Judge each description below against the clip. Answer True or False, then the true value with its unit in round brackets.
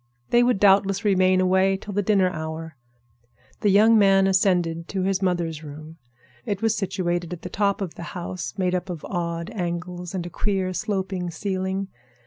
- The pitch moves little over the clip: True (2.2 semitones)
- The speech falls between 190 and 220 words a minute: False (175 wpm)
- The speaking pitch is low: False (185 Hz)